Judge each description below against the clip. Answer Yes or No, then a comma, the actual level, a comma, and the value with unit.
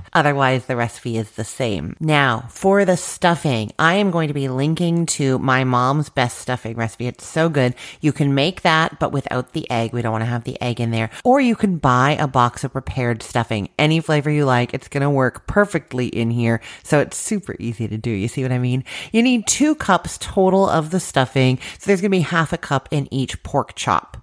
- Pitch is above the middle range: No, low, 135 Hz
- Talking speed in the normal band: No, fast, 230 wpm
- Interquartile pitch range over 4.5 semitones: Yes, average, 5.2 semitones